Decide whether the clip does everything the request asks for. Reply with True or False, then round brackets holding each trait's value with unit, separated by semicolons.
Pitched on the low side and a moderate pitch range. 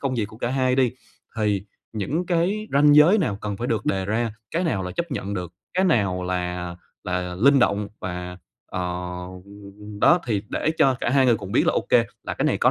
False (110 Hz; 6.8 semitones)